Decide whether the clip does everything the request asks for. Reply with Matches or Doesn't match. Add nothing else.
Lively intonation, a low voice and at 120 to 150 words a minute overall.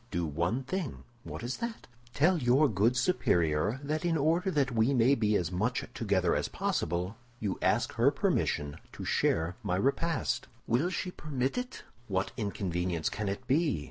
Doesn't match